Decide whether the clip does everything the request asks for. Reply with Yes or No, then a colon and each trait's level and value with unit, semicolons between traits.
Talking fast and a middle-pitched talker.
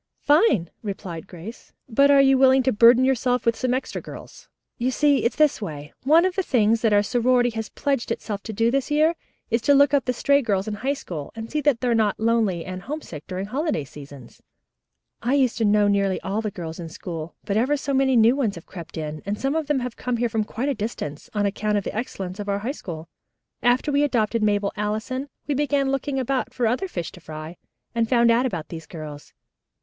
No: fast, 230 wpm; high, 230 Hz